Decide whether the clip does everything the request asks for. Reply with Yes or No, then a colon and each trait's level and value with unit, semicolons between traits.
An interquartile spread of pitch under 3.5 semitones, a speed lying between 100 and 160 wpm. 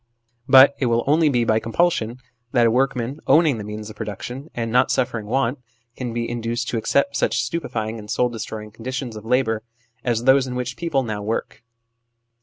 No: average, 2.9 semitones; average, 190 wpm